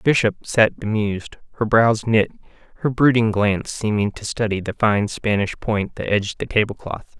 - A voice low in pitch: Yes, low, 110 Hz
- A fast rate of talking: No, average, 175 wpm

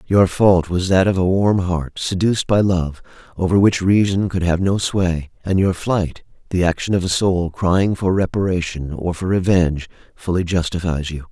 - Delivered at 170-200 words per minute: Yes, average, 185 wpm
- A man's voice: Yes, male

